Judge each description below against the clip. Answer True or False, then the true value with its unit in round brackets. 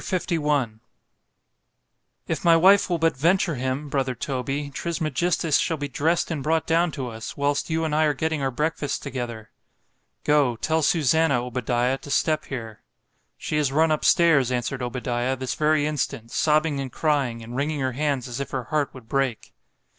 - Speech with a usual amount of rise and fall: True (3.5 semitones)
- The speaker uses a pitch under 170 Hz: True (140 Hz)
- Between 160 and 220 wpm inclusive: True (170 wpm)